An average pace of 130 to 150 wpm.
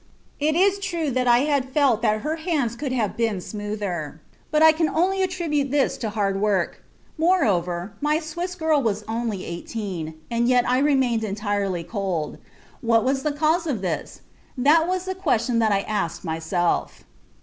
No: average, 170 wpm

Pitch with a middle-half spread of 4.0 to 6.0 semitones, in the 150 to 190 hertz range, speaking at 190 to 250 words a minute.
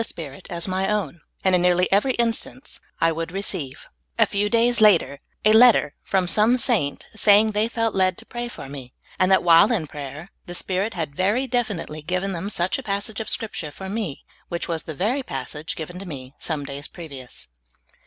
Yes: average, 5.3 semitones; medium, 185 Hz; average, 200 wpm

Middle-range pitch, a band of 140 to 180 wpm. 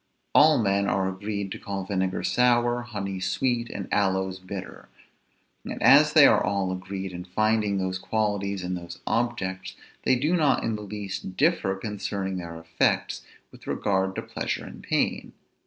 No: low, 100 Hz; average, 160 wpm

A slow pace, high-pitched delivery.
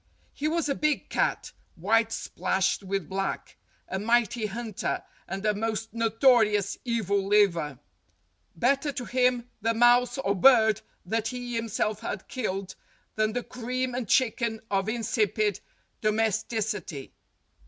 Yes: slow, 130 wpm; high, 225 Hz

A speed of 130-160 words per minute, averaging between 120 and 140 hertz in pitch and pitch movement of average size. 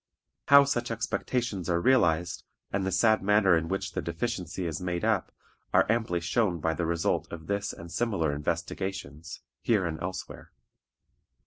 No: average, 155 wpm; very low, 90 Hz; average, 4.5 semitones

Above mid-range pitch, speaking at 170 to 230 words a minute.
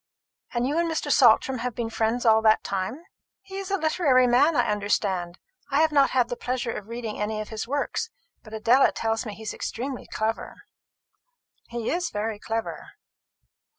Yes: high, 235 Hz; average, 185 wpm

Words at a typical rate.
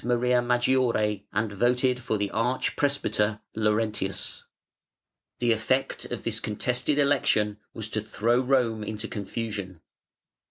No: slow, 120 wpm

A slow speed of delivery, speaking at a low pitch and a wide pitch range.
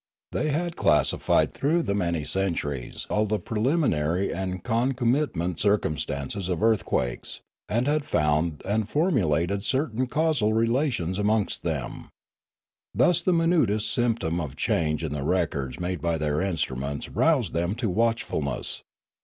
Yes: slow, 130 wpm; low, 100 Hz; wide, 7.0 semitones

